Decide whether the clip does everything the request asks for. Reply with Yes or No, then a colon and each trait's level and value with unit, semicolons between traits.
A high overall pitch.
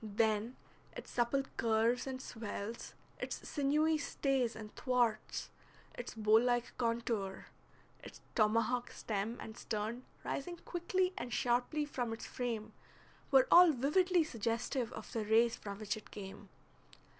Yes: high, 235 Hz